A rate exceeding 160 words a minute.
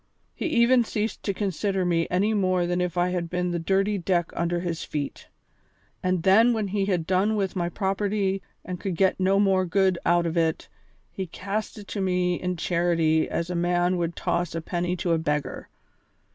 Yes: average, 200 wpm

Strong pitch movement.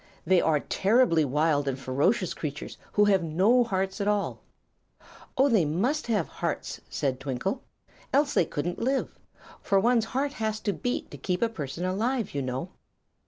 Yes: wide, 7.1 semitones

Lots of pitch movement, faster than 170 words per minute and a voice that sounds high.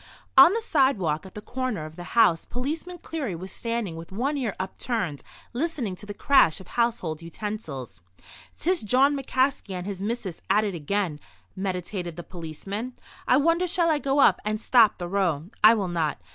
Yes: wide, 6.9 semitones; average, 180 wpm; high, 210 Hz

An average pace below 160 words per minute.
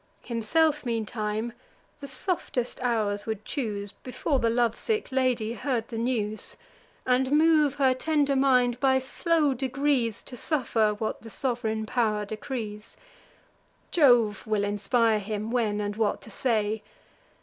Yes: slow, 135 wpm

